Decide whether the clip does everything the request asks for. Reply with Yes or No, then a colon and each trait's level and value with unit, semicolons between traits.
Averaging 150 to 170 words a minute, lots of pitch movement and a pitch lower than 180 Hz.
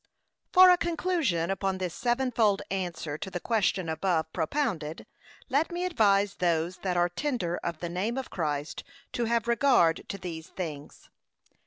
No: average, 155 wpm; wide, 6.2 semitones; high, 190 Hz